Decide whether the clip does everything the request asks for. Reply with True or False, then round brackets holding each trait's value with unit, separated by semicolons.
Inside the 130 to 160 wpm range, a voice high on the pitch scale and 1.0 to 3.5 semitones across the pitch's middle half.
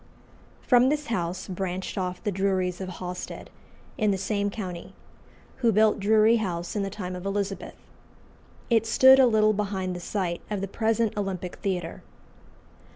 True (155 wpm; 195 Hz; 2.9 semitones)